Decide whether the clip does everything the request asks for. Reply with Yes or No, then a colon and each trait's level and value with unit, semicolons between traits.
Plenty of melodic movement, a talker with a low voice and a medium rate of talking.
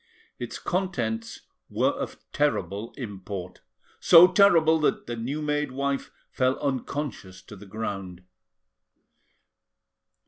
No: wide, 6.5 semitones; low, 130 Hz; slow, 105 wpm